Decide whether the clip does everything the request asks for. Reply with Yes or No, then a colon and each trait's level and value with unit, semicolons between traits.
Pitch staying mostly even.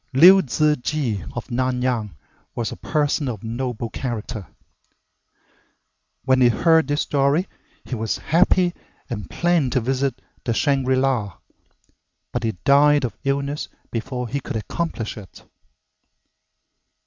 No: average, 3.8 semitones